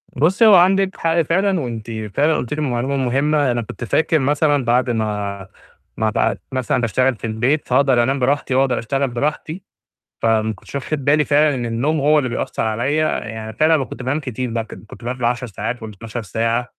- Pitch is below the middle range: Yes, low, 130 Hz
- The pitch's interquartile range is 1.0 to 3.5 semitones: No, average, 4.3 semitones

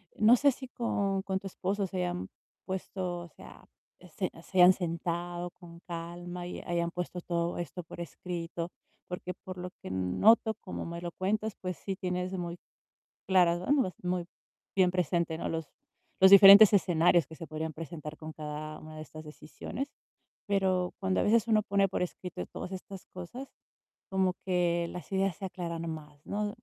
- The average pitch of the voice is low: No, medium, 180 Hz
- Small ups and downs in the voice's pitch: Yes, narrow, 2.1 semitones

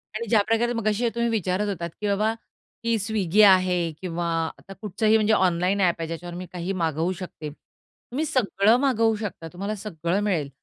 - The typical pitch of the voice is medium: No, high, 200 Hz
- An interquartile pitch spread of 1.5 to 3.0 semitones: No, average, 3.8 semitones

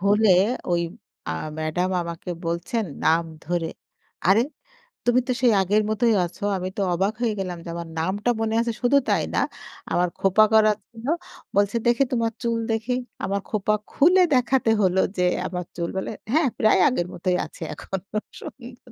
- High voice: Yes, high, 205 Hz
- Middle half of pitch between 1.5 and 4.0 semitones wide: No, average, 4.6 semitones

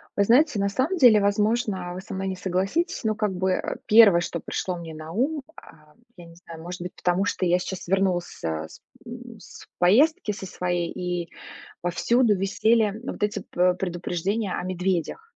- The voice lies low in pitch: No, high, 190 Hz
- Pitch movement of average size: Yes, average, 3.6 semitones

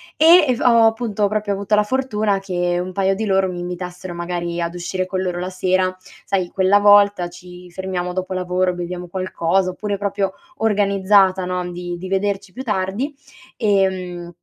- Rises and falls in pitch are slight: Yes, narrow, 2.2 semitones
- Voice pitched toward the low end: No, high, 190 Hz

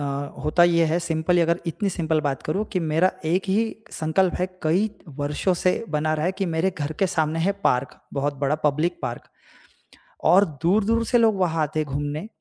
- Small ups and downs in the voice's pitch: No, average, 3.4 semitones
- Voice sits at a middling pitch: Yes, medium, 165 Hz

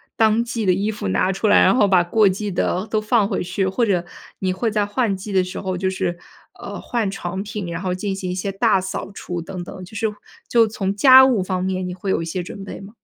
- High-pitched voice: Yes, high, 195 Hz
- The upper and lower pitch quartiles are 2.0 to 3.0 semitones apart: Yes, narrow, 2.5 semitones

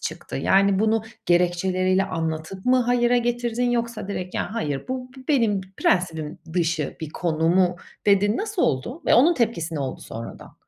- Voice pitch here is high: Yes, high, 195 Hz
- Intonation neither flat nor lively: No, wide, 6.1 semitones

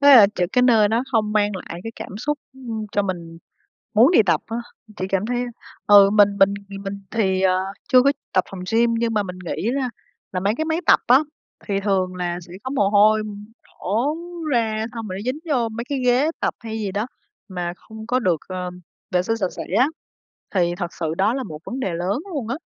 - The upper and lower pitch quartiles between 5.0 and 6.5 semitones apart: No, average, 4.1 semitones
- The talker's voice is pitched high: Yes, high, 210 Hz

